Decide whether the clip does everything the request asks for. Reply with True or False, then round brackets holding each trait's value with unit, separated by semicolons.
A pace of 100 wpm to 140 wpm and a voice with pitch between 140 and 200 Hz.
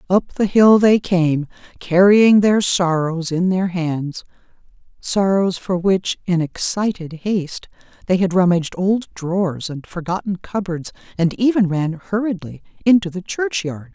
True (135 wpm; 185 Hz)